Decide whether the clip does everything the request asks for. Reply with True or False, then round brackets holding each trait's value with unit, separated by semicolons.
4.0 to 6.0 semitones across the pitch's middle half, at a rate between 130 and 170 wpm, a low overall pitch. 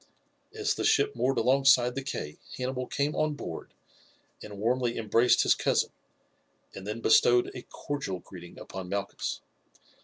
True (4.8 semitones; 145 wpm; 125 Hz)